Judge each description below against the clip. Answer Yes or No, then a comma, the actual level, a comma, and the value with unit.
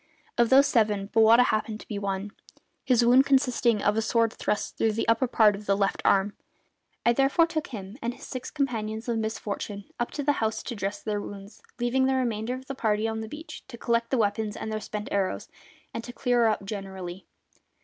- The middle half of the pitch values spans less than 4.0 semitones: Yes, average, 3.0 semitones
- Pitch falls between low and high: No, high, 225 Hz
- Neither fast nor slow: No, fast, 210 wpm